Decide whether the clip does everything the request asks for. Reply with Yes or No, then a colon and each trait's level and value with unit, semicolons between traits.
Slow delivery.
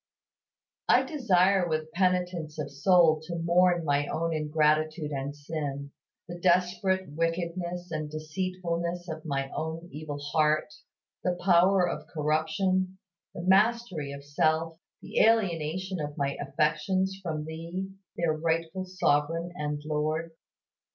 Yes: slow, 125 wpm